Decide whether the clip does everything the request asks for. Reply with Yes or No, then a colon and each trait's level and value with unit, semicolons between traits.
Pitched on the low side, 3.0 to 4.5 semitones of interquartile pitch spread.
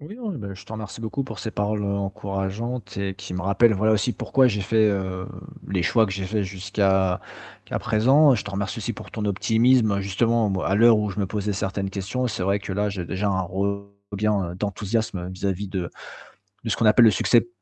No: low, 100 Hz; narrow, 2.5 semitones